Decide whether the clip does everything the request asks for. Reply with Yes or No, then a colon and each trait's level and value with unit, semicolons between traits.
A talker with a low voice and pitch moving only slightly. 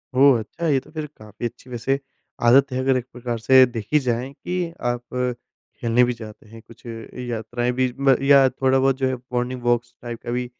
Yes: low, 125 Hz; narrow, 1.9 semitones